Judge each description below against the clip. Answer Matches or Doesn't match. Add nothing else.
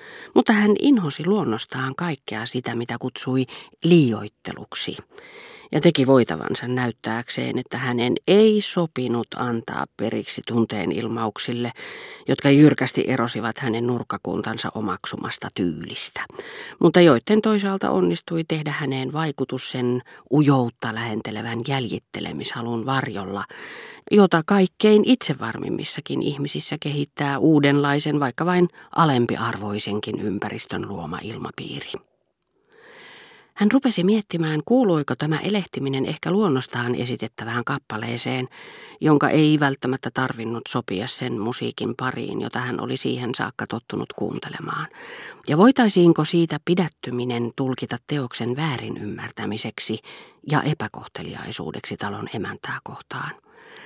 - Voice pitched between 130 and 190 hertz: Matches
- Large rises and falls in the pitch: Matches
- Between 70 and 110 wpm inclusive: Matches